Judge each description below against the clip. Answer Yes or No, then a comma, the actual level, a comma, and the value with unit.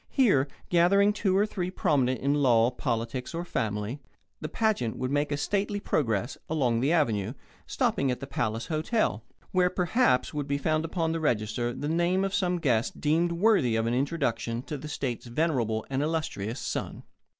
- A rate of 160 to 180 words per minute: Yes, average, 175 wpm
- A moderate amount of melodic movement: No, wide, 6.1 semitones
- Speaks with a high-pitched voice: No, medium, 145 Hz